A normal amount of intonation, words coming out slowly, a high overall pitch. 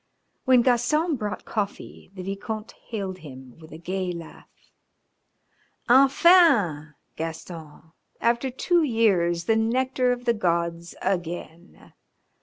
No: wide, 6.4 semitones; slow, 110 wpm; high, 200 Hz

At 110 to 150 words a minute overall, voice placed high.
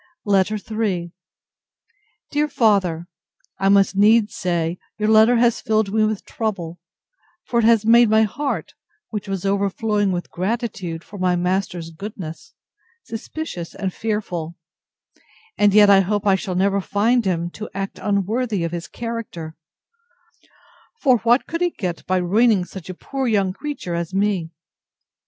Yes: average, 145 wpm; high, 200 Hz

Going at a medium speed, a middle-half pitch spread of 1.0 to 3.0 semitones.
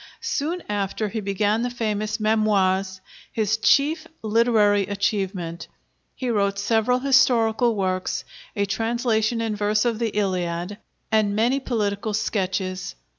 No: slow, 125 wpm; narrow, 2.6 semitones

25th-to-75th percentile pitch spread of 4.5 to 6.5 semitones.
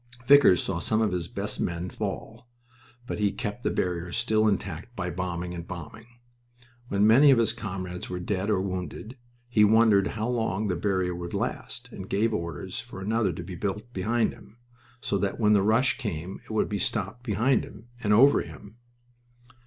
No: average, 3.6 semitones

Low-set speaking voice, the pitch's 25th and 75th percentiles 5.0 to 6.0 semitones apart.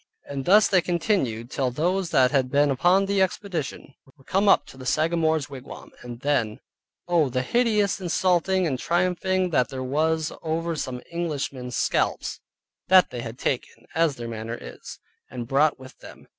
No: medium, 155 Hz; wide, 5.6 semitones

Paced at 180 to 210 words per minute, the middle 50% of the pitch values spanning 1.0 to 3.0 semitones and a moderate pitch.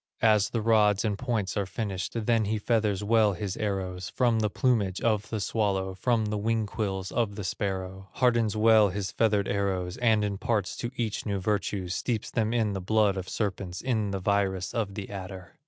No: average, 190 wpm; narrow, 2.5 semitones; low, 105 Hz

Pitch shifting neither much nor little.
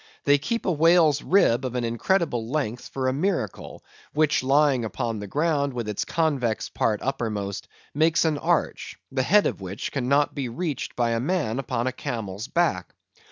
Yes: average, 5.0 semitones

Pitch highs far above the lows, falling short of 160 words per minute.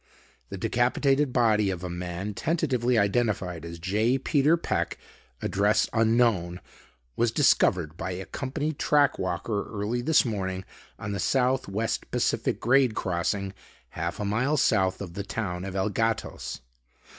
No: average, 4.9 semitones; average, 145 wpm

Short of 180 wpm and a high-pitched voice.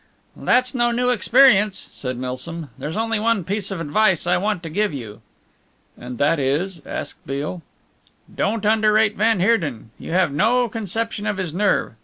Yes: average, 165 wpm; high, 195 Hz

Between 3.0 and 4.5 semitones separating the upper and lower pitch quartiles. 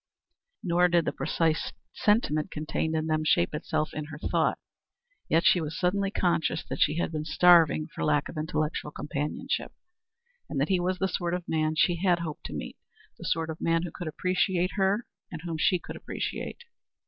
No: narrow, 2.5 semitones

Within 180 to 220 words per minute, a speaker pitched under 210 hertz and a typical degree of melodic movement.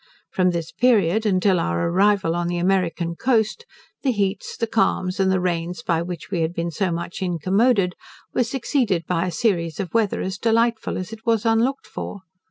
Yes: average, 185 wpm; high, 190 Hz; average, 4.5 semitones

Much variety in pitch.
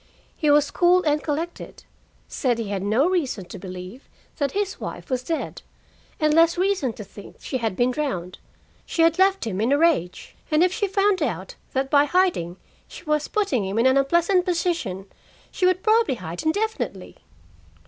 Yes: wide, 7.9 semitones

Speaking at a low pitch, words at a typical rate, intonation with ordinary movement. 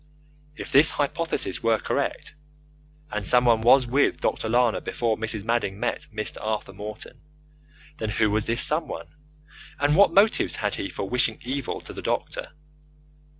Yes: low, 115 Hz; average, 150 wpm; average, 4.2 semitones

